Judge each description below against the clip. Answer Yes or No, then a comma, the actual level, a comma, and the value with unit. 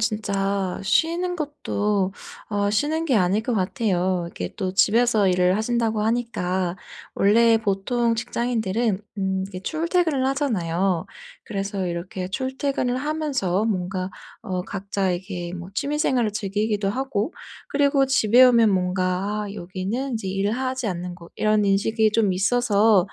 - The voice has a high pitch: Yes, high, 210 Hz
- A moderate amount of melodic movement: Yes, average, 4.4 semitones